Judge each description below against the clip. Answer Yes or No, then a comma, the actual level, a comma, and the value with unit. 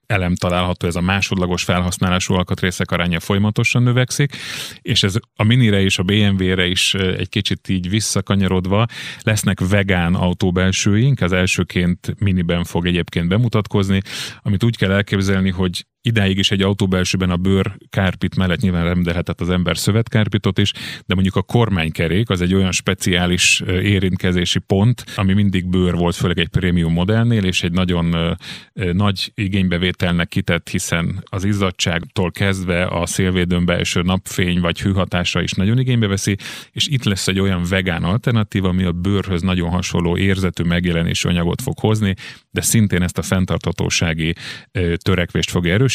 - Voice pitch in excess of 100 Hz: No, very low, 95 Hz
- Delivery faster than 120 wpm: Yes, average, 150 wpm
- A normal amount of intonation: No, narrow, 2.3 semitones